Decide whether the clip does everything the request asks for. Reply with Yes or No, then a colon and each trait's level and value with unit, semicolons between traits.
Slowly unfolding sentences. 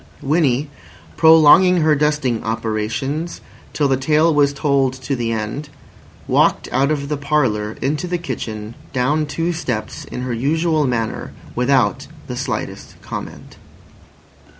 Yes: slow, 130 wpm